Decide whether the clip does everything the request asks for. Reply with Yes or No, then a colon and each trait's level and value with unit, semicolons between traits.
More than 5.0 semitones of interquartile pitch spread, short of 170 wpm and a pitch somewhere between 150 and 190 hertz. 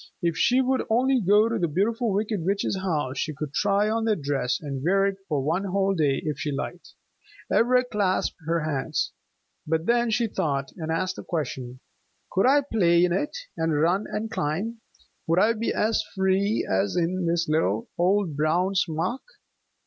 No: wide, 5.5 semitones; average, 180 wpm; medium, 185 Hz